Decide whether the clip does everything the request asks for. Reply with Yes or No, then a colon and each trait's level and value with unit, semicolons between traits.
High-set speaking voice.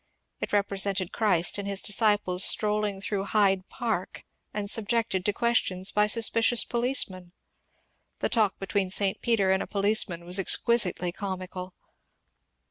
Yes: high, 200 Hz